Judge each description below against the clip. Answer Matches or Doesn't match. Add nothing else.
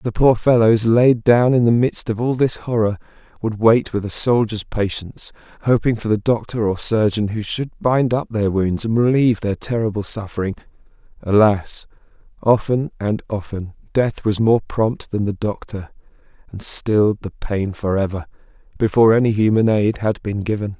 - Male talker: Matches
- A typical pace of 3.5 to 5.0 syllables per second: Matches